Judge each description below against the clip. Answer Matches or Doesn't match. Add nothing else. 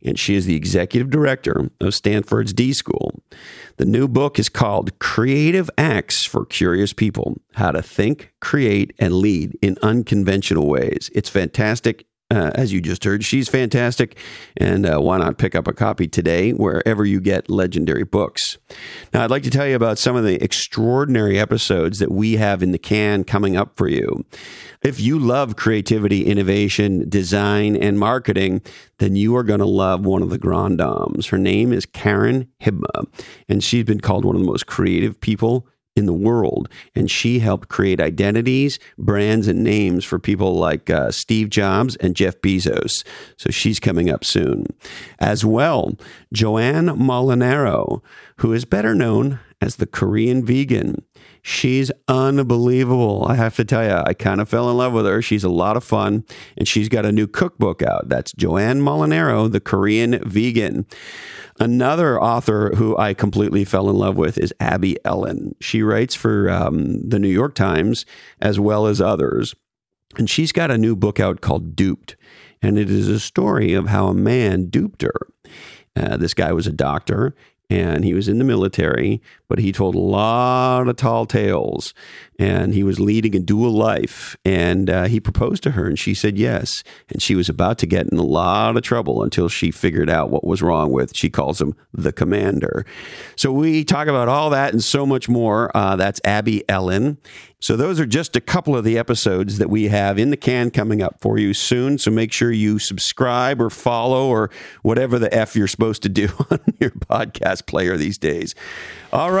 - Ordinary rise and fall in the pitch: Matches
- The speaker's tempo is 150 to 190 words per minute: Matches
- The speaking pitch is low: Matches